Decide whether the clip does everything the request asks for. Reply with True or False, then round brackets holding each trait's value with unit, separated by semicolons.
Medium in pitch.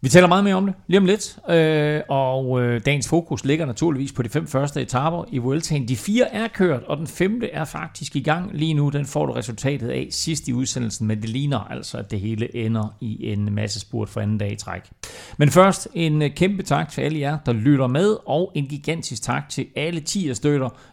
True (145 Hz)